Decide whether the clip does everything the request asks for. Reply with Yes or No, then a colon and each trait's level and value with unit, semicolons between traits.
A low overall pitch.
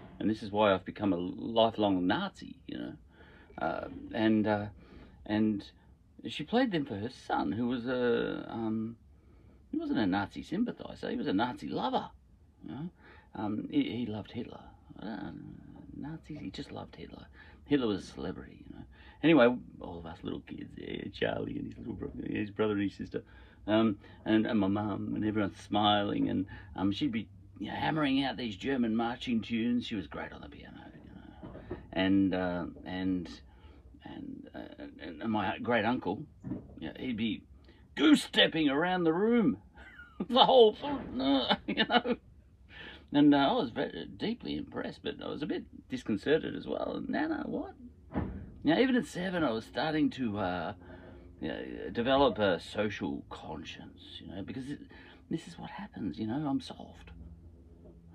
Yes: low, 110 Hz